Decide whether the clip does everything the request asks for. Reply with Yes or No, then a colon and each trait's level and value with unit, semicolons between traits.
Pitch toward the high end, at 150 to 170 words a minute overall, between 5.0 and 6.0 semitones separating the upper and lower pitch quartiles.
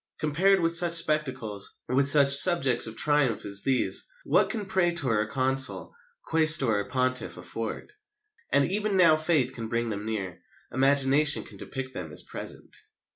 No: low, 135 Hz; average, 155 wpm; average, 5.3 semitones